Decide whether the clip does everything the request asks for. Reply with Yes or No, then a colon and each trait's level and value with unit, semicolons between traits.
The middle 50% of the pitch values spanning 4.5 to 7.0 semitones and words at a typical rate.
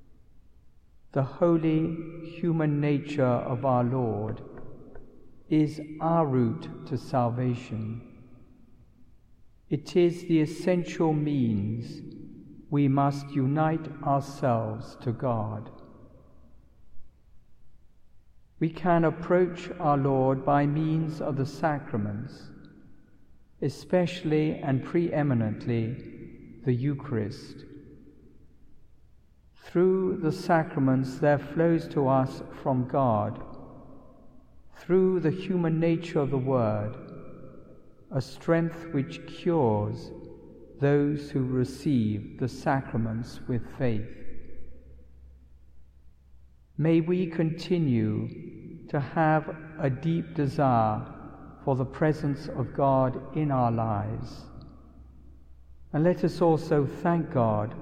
No: wide, 5.6 semitones; slow, 90 wpm